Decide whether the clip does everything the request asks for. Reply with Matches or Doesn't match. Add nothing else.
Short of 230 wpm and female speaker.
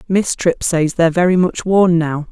Matches